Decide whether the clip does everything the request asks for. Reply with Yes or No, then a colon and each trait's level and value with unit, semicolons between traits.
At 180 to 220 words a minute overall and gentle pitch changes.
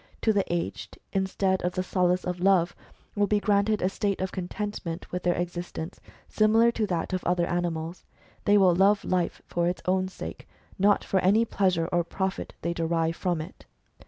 Yes: average, 185 wpm; narrow, 2.3 semitones